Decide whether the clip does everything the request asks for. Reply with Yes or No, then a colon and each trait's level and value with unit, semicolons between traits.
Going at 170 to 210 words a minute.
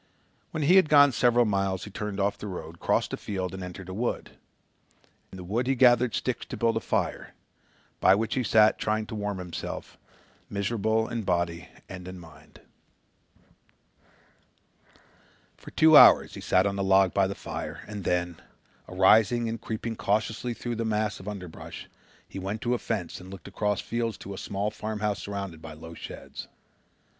Yes: average, 180 wpm